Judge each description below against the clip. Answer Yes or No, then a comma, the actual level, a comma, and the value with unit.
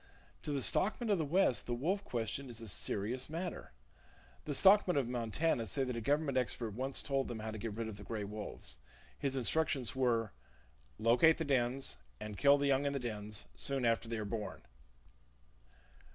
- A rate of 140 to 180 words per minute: No, average, 190 wpm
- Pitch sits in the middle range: No, low, 125 Hz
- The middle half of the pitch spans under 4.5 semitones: Yes, average, 4.1 semitones